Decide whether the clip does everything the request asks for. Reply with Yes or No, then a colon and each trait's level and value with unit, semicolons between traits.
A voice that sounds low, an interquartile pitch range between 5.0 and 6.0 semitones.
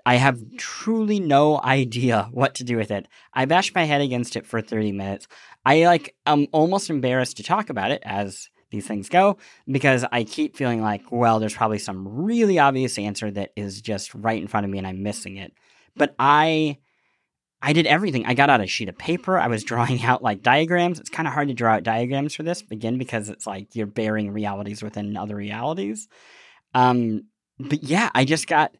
Yes: low, 120 Hz; wide, 5.6 semitones